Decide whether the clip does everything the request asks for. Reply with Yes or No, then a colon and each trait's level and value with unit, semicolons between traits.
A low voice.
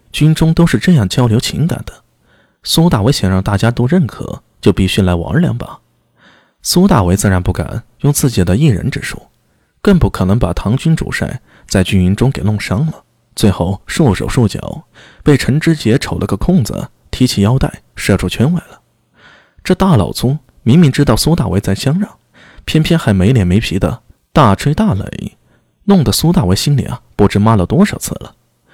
Yes: low, 115 Hz